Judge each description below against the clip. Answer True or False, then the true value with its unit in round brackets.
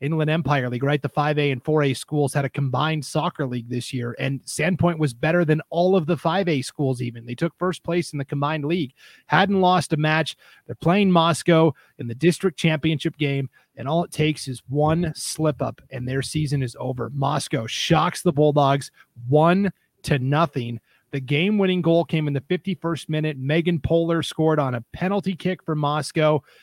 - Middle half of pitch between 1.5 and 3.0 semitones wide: False (3.4 semitones)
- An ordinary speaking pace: True (190 wpm)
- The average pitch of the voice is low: False (155 Hz)